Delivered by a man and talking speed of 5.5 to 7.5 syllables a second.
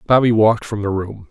Yes: male; 6.0 syllables/s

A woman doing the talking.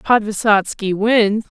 Yes: female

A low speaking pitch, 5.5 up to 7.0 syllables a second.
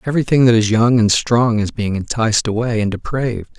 Yes: low, 115 Hz; 5.9 syllables/s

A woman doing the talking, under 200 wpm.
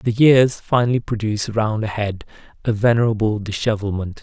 No: male; average, 140 wpm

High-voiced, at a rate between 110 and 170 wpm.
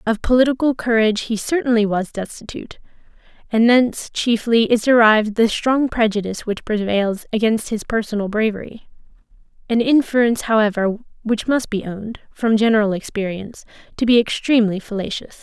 Yes: high, 220 Hz; slow, 135 wpm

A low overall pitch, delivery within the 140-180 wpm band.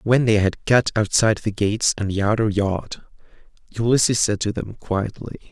Yes: low, 105 Hz; average, 175 wpm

